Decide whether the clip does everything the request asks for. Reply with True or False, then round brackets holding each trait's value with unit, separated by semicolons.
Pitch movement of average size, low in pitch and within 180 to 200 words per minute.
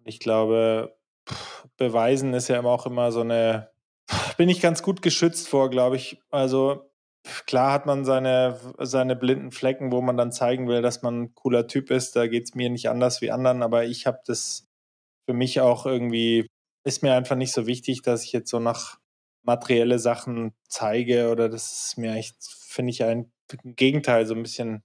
False (2.0 semitones; 120 Hz; 190 wpm)